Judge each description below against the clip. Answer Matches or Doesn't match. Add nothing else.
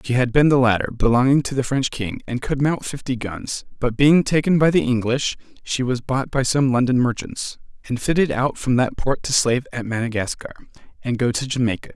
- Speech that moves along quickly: Matches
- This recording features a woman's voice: Doesn't match